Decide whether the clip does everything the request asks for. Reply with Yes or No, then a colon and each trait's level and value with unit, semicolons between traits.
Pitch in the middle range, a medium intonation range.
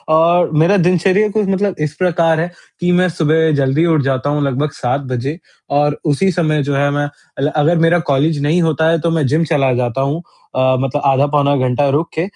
Yes: medium, 155 Hz; average, 3.1 semitones